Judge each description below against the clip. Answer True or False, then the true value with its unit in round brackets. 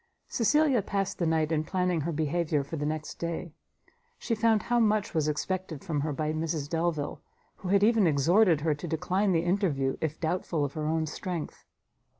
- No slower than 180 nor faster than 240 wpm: True (185 wpm)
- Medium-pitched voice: True (165 Hz)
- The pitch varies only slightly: False (3.8 semitones)